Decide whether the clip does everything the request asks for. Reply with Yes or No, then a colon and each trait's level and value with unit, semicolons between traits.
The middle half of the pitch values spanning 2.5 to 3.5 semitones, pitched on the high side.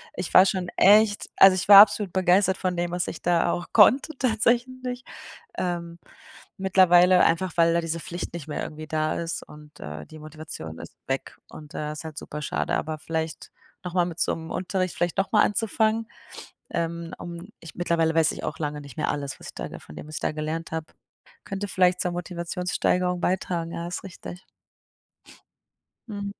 No: average, 2.8 semitones; medium, 175 Hz